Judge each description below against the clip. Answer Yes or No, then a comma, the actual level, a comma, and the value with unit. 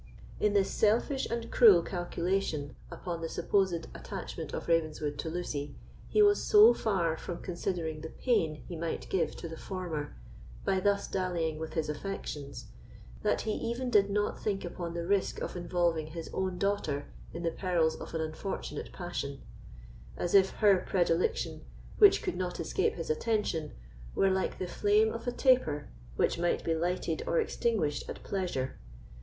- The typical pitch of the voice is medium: Yes, medium, 180 Hz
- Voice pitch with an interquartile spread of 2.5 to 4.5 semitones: Yes, average, 3.8 semitones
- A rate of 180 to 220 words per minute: No, average, 165 wpm